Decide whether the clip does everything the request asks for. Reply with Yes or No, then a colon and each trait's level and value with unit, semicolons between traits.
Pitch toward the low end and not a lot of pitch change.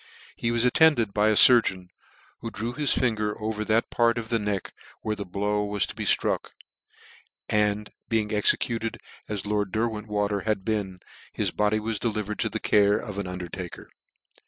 Yes: low, 105 Hz; narrow, 1.7 semitones